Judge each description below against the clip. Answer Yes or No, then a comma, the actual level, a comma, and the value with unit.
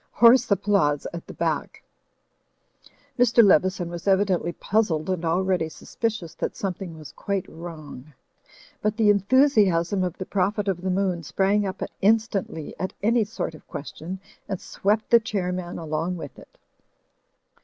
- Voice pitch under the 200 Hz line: Yes, high, 190 Hz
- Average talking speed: Yes, average, 150 wpm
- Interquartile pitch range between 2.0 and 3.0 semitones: No, average, 3.5 semitones